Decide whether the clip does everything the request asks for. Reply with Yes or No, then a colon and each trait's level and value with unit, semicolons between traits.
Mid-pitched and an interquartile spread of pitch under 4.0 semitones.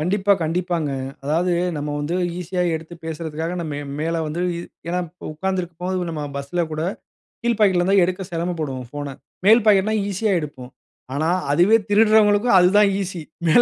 Yes: medium, 175 Hz; average, 3.6 semitones